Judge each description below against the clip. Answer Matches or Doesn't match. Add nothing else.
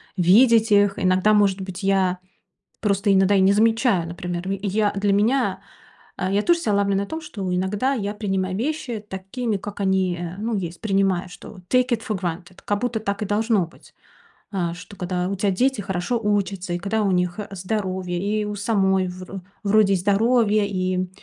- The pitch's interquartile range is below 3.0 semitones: Matches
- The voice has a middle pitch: Doesn't match